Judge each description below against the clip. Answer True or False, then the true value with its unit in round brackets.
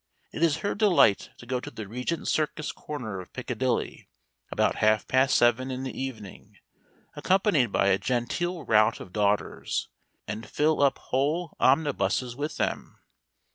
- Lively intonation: True (5.7 semitones)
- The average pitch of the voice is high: False (130 Hz)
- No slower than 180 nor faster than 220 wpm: False (150 wpm)